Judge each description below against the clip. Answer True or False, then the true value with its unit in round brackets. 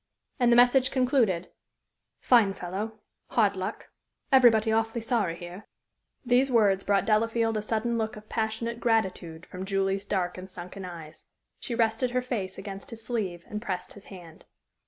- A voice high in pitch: True (220 Hz)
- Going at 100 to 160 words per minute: True (155 wpm)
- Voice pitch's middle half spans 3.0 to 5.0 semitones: True (3.7 semitones)